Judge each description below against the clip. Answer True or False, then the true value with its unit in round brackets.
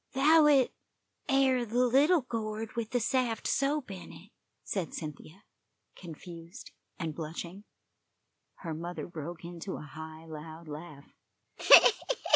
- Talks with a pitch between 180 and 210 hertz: True (185 Hz)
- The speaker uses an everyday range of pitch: False (7.3 semitones)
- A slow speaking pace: True (120 wpm)